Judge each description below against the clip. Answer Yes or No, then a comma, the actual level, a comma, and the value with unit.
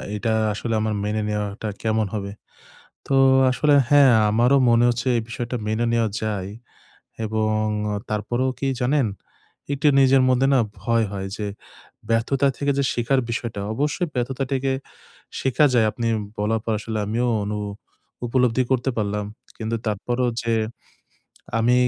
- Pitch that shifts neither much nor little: Yes, average, 3.1 semitones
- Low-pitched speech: Yes, low, 115 Hz